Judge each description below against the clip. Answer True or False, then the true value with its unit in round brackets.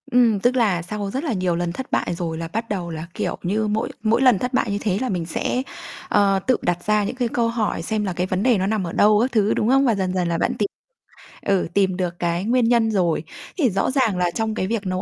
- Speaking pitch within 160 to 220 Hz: True (205 Hz)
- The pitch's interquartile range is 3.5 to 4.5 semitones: True (4.2 semitones)